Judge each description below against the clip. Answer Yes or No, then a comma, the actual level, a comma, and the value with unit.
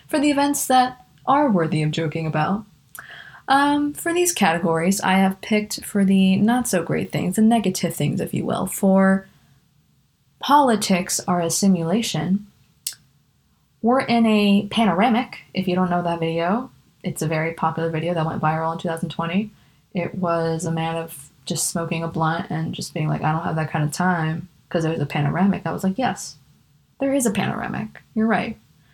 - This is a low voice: No, medium, 180 Hz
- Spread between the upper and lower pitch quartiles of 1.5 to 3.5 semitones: No, average, 4.8 semitones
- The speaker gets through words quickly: No, average, 180 wpm